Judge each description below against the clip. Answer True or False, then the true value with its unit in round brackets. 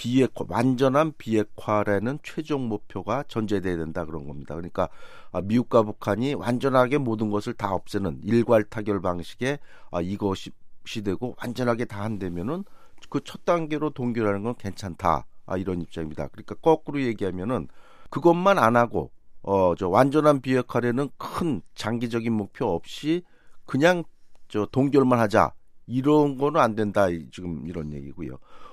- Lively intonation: True (5.7 semitones)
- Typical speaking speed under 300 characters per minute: False (310 characters per minute)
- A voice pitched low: True (115 Hz)